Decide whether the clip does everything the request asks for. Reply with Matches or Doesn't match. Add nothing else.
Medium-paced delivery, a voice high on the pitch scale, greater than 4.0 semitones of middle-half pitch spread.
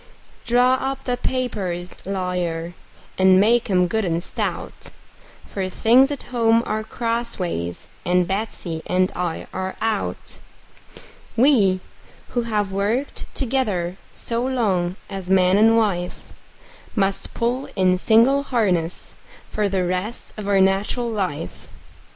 Doesn't match